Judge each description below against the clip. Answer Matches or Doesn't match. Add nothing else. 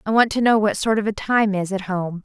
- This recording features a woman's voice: Matches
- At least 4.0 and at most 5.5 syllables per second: Doesn't match